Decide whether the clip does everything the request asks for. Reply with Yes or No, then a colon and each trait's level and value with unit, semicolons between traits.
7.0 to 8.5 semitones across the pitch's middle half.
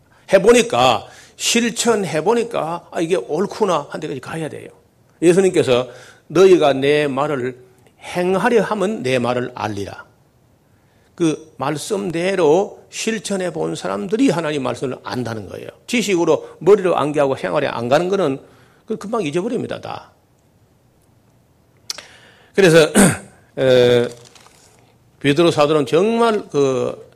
Yes: wide, 8.0 semitones